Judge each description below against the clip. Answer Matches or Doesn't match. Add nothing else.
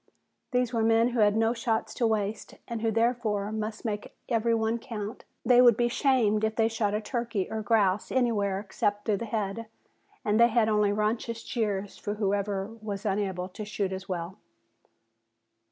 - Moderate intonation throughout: Doesn't match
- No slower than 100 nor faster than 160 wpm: Doesn't match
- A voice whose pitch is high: Matches